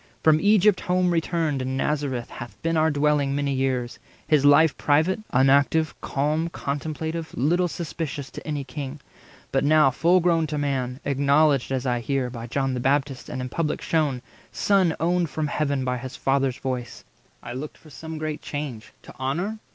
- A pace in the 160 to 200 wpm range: Yes, average, 175 wpm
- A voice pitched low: No, medium, 145 Hz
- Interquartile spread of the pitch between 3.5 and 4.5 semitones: No, average, 3.1 semitones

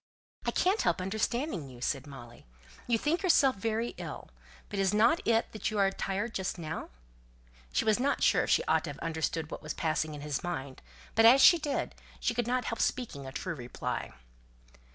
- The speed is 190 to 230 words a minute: Yes, average, 195 wpm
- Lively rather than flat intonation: Yes, wide, 7.6 semitones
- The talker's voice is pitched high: Yes, high, 200 Hz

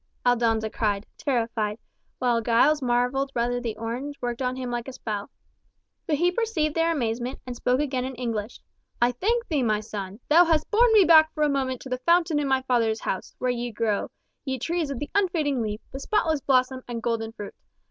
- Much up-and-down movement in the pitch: No, average, 4.4 semitones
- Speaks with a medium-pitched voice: No, very high, 255 Hz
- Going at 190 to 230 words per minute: Yes, average, 200 wpm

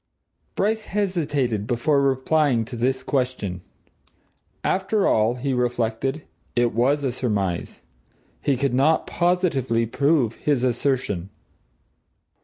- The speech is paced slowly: Yes, slow, 105 wpm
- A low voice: Yes, low, 130 Hz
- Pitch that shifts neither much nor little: Yes, average, 4.0 semitones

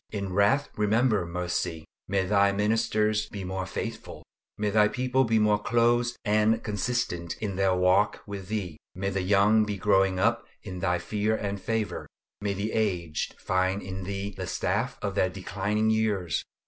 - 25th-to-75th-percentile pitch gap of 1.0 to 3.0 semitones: Yes, narrow, 2.5 semitones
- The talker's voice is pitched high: No, low, 100 Hz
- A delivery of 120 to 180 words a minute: Yes, average, 165 wpm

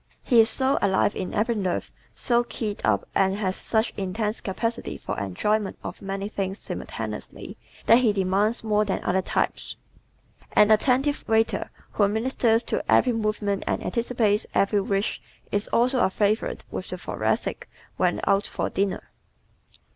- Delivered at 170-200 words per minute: No, average, 155 wpm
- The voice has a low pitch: No, high, 210 Hz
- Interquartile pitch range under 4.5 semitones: Yes, narrow, 2.6 semitones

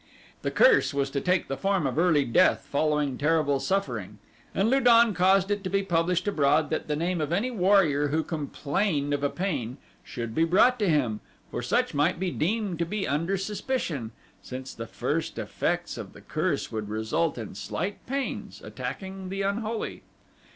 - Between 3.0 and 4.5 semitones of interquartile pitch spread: No, wide, 5.4 semitones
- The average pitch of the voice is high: No, medium, 170 Hz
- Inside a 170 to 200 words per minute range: Yes, average, 180 wpm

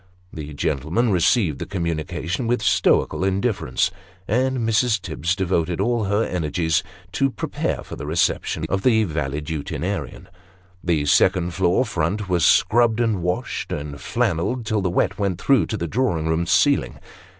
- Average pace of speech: Yes, average, 150 wpm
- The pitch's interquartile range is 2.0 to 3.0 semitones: No, average, 5.3 semitones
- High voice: No, very low, 90 Hz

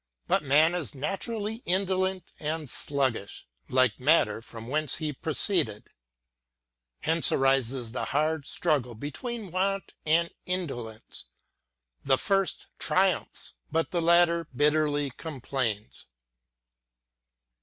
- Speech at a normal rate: No, slow, 110 wpm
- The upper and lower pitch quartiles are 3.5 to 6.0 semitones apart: Yes, average, 5.0 semitones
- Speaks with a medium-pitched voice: Yes, medium, 150 Hz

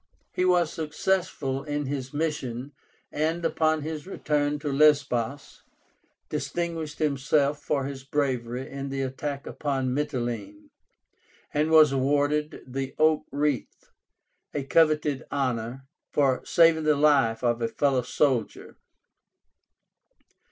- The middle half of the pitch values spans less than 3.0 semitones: Yes, narrow, 2.5 semitones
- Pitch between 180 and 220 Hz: No, medium, 145 Hz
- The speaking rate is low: Yes, slow, 115 wpm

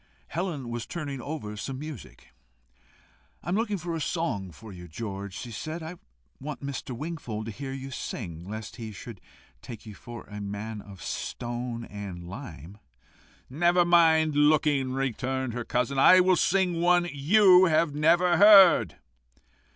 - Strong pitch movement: Yes, wide, 7.4 semitones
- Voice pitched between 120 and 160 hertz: Yes, low, 135 Hz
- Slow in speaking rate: No, average, 155 wpm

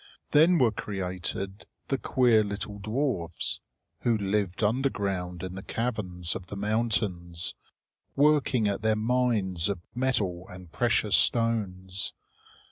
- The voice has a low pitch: Yes, low, 105 Hz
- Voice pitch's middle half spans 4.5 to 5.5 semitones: No, average, 4.1 semitones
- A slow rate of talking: Yes, slow, 120 wpm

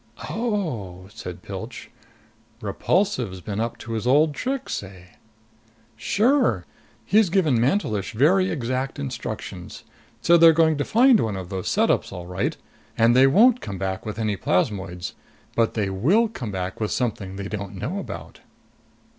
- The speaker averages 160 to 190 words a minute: No, average, 150 wpm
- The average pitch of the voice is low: Yes, low, 115 Hz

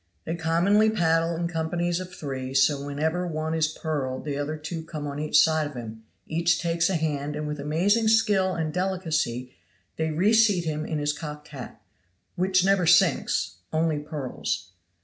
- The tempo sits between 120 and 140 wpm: No, average, 175 wpm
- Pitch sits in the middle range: Yes, medium, 160 Hz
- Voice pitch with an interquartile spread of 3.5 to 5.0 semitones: No, average, 2.9 semitones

